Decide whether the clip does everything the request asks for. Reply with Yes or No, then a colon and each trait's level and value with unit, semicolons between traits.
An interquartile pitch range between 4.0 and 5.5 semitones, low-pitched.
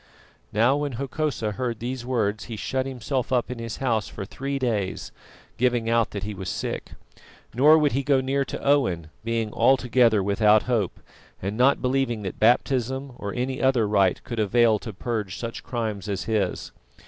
No: average, 3.6 semitones; low, 115 Hz